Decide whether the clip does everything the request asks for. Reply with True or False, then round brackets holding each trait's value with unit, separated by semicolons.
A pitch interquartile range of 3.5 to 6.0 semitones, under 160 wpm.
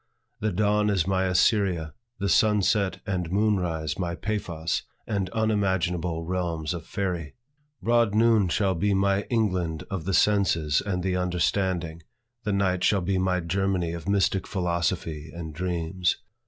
False (2.8 semitones; 150 wpm)